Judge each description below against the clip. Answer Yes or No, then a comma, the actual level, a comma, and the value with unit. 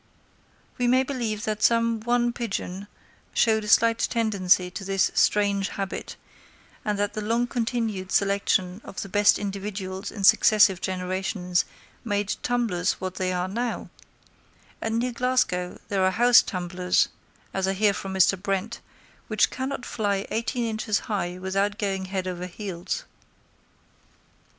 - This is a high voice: Yes, high, 205 Hz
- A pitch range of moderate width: Yes, average, 3.3 semitones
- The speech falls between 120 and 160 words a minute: Yes, average, 140 wpm